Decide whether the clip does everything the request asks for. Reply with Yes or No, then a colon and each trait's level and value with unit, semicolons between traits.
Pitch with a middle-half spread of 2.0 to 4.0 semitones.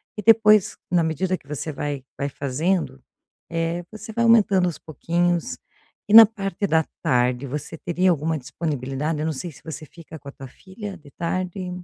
No: average, 4.4 semitones